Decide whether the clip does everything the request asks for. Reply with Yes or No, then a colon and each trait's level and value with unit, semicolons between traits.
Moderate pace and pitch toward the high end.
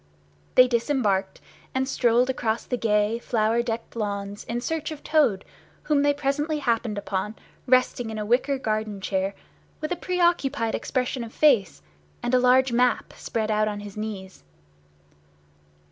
Yes: average, 155 wpm; high, 235 Hz